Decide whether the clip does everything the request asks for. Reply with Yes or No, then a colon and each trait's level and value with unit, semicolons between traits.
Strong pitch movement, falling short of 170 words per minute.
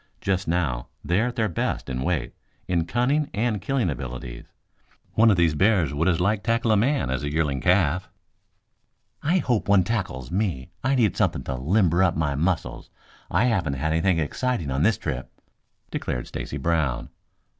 No: wide, 6.9 semitones; average, 175 wpm